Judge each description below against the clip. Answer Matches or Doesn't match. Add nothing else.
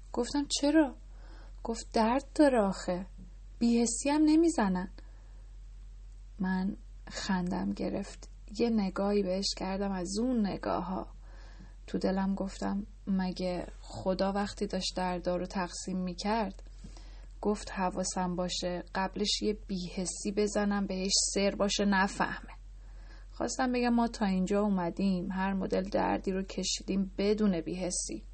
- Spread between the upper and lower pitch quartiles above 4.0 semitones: Doesn't match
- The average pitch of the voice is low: Doesn't match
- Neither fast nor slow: Matches